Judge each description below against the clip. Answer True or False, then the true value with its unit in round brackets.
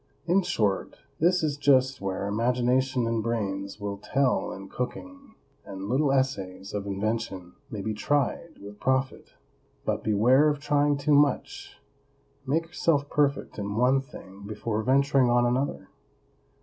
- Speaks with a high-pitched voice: False (125 Hz)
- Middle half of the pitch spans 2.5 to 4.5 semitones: False (5.6 semitones)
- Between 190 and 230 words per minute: False (140 wpm)